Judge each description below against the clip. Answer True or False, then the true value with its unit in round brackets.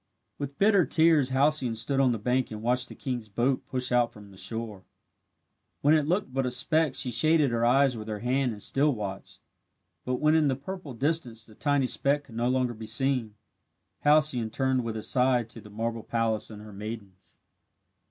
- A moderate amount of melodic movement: True (3.7 semitones)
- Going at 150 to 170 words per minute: False (195 wpm)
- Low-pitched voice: True (125 Hz)